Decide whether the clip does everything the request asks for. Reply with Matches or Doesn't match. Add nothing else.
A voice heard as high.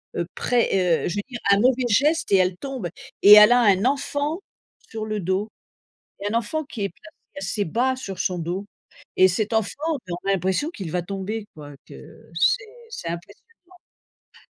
Matches